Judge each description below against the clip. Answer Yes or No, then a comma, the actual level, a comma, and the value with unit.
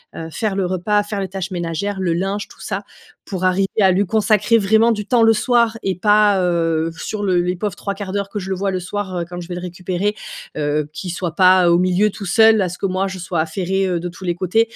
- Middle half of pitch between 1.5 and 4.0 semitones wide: Yes, narrow, 2.6 semitones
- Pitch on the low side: No, high, 190 Hz